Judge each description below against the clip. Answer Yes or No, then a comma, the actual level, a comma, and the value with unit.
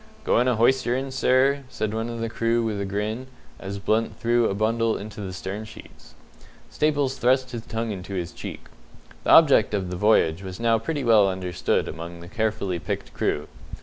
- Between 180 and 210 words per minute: Yes, average, 185 wpm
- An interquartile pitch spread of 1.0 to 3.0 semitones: No, average, 3.5 semitones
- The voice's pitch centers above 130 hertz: No, low, 110 Hz